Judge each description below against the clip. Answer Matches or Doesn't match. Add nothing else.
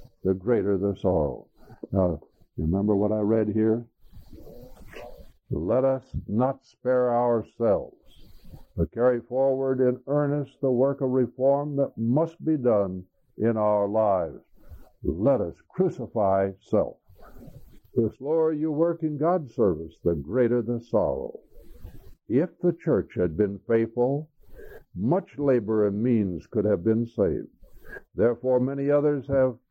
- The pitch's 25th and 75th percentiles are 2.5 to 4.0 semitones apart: Doesn't match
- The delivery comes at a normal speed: Doesn't match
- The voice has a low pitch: Matches